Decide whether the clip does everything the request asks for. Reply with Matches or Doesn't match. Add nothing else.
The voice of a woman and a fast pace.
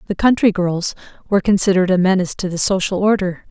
Doesn't match